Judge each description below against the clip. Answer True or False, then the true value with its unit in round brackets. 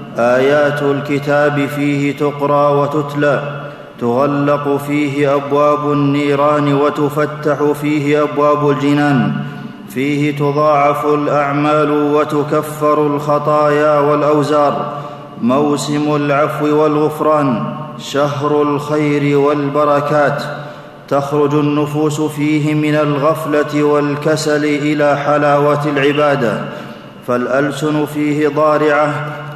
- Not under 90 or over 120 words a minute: False (75 wpm)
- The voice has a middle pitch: True (145 Hz)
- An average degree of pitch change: False (0.6 semitones)